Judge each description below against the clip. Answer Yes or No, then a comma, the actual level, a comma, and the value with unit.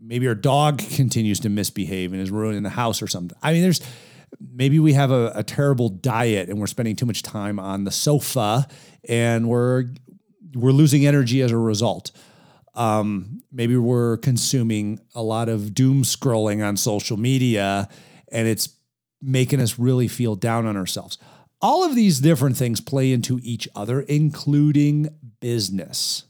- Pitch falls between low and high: No, low, 120 Hz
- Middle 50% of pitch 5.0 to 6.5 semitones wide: No, average, 4.2 semitones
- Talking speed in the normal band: Yes, average, 165 wpm